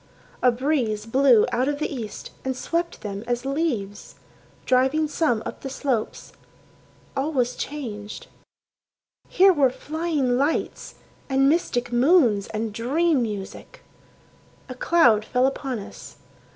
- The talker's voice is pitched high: Yes, very high, 255 Hz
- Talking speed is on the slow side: Yes, slow, 125 wpm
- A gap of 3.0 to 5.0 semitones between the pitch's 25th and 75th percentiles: Yes, average, 4.4 semitones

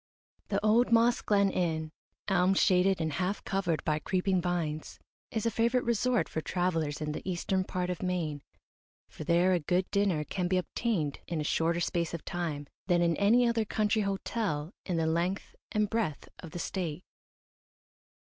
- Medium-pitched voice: Yes, medium, 180 Hz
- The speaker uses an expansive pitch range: No, average, 3.7 semitones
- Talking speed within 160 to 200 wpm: Yes, average, 175 wpm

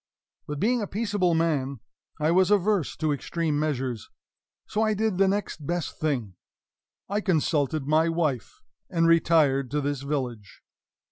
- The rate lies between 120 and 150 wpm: Yes, average, 140 wpm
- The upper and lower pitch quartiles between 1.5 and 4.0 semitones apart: No, average, 4.6 semitones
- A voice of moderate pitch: Yes, medium, 155 Hz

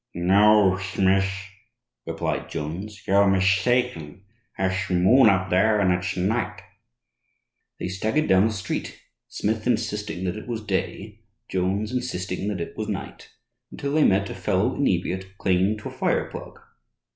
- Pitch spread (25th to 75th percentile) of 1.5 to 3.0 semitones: Yes, narrow, 2.5 semitones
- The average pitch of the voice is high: No, very low, 95 Hz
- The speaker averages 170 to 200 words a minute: No, average, 145 wpm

